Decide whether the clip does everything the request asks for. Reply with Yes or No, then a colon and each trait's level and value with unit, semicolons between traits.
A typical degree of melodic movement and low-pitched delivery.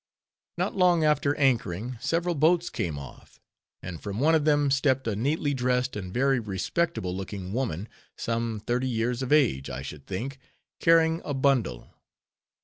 No: wide, 6.3 semitones; low, 125 Hz